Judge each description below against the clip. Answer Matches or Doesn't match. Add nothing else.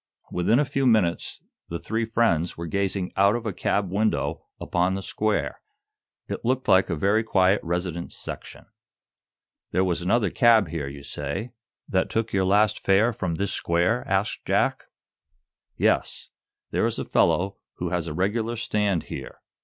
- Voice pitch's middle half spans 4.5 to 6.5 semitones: Doesn't match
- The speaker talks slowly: Doesn't match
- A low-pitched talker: Matches